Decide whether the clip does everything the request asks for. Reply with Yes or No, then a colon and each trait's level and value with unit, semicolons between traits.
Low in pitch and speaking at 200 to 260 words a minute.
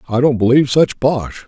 Yes: low, 130 Hz; fast, 205 wpm